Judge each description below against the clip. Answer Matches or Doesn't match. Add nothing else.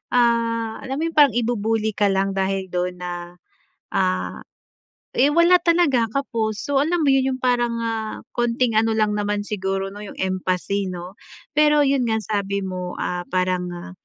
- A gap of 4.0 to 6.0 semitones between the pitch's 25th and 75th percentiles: Matches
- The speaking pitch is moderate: Doesn't match